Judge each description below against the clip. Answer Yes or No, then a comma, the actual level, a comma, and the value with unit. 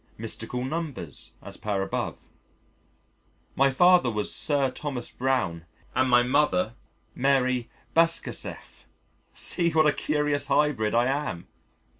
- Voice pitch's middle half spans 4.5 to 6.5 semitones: No, average, 4.0 semitones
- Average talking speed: No, slow, 115 wpm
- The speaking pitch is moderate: No, low, 130 Hz